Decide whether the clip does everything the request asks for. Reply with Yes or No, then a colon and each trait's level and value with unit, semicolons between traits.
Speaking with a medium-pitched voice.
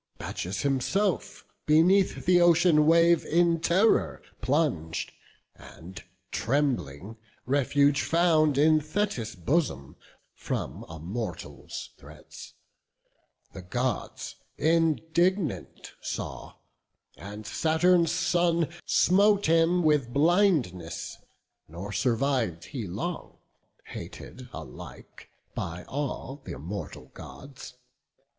Yes: medium, 145 Hz